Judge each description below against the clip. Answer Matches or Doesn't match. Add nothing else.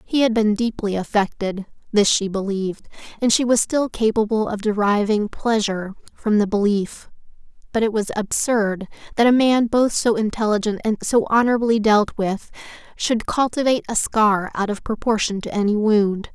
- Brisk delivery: Doesn't match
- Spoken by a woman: Matches